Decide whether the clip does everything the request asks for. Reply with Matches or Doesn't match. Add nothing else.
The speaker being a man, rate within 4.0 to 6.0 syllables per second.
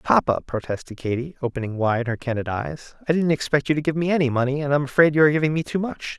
Doesn't match